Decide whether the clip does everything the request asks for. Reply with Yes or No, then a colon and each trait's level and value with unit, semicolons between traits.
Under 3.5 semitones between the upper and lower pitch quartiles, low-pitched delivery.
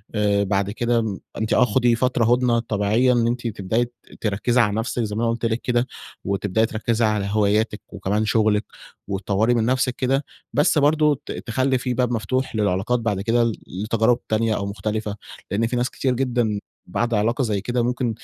Yes: average, 2.7 semitones; low, 115 Hz